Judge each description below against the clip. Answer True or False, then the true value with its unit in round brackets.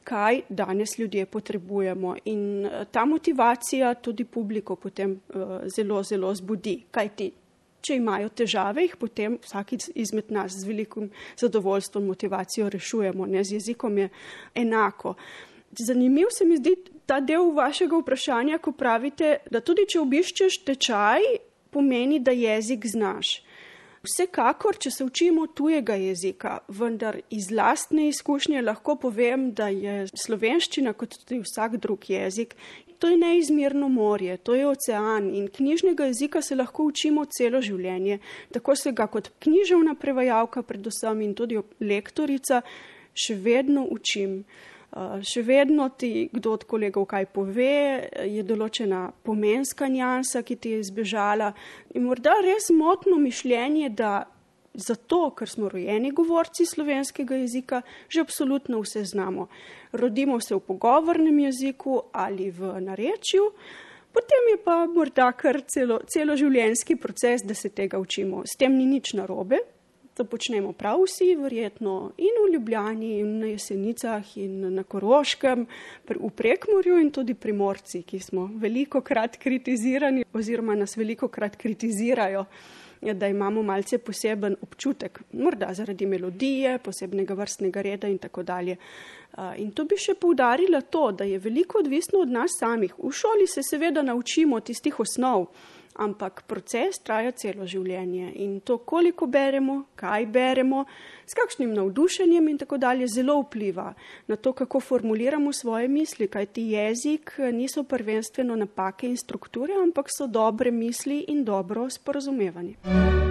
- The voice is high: True (240 Hz)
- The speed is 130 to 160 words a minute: True (140 wpm)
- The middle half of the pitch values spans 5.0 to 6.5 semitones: True (5.5 semitones)